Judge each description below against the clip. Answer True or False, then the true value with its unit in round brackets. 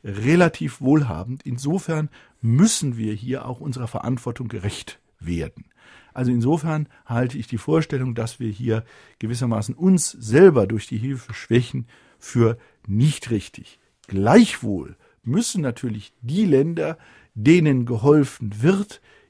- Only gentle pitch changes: False (4.9 semitones)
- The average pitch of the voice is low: True (125 Hz)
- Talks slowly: True (120 wpm)